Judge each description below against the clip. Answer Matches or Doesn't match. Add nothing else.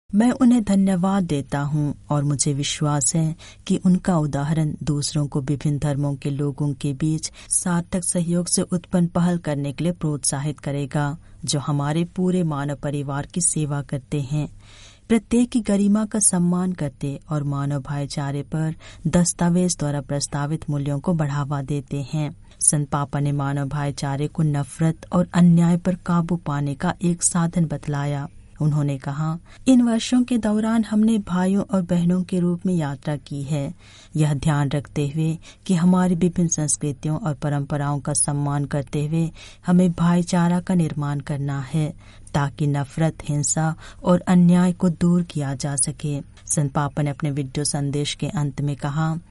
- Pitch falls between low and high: Matches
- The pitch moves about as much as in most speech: Matches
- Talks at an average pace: Matches